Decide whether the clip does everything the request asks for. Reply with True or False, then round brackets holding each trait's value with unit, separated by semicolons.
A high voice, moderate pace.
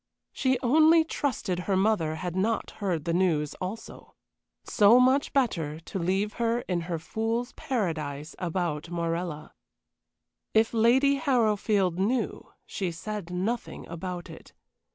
False (195 Hz; 130 wpm)